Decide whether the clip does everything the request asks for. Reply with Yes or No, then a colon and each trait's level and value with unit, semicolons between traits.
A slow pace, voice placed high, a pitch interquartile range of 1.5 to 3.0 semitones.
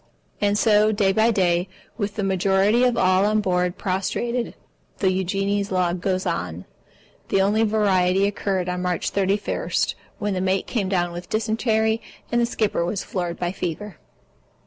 No: average, 160 wpm; high, 195 Hz; narrow, 2.5 semitones